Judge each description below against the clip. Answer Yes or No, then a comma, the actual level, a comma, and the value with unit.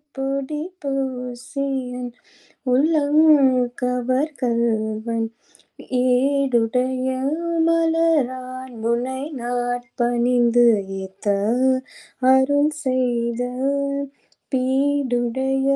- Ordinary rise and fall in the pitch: No, narrow, 2.2 semitones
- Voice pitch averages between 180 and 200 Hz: No, very high, 255 Hz